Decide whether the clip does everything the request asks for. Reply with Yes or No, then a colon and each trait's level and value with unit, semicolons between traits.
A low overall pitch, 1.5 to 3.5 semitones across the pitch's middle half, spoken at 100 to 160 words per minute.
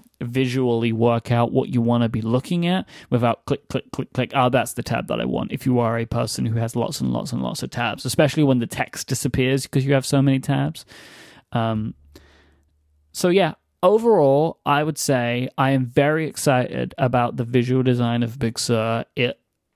No: low, 125 Hz; average, 3.0 semitones; average, 200 wpm